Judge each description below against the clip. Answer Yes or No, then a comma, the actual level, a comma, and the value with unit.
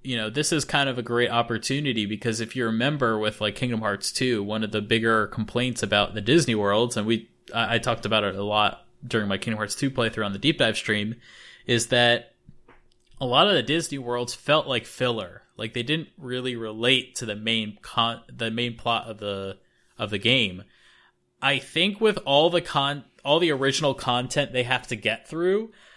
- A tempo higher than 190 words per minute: Yes, fast, 205 wpm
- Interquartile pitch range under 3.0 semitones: No, average, 3.6 semitones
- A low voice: Yes, low, 120 Hz